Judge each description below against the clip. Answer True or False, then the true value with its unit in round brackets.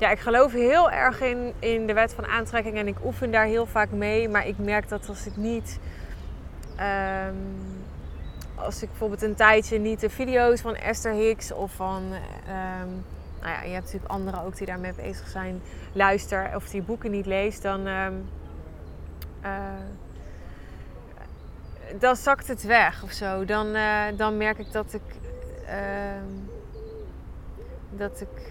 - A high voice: True (200 Hz)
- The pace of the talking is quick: False (160 wpm)